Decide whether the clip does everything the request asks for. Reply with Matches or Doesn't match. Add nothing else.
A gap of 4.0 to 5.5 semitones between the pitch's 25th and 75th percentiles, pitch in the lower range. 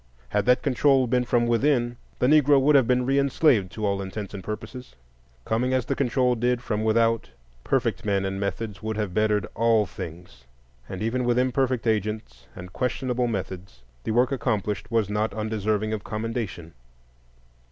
Doesn't match